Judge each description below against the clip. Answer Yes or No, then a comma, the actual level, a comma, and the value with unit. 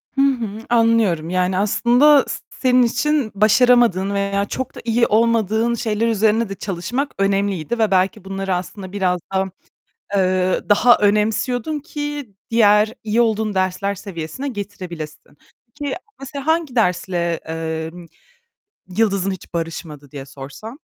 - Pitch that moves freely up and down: No, average, 4.3 semitones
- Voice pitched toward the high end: Yes, high, 205 Hz